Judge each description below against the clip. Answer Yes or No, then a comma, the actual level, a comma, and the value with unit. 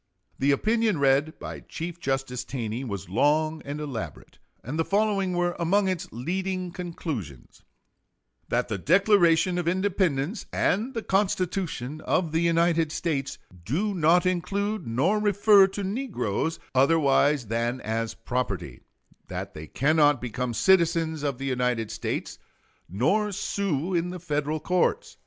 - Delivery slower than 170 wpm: Yes, slow, 135 wpm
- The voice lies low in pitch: No, medium, 160 Hz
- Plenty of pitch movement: Yes, wide, 5.8 semitones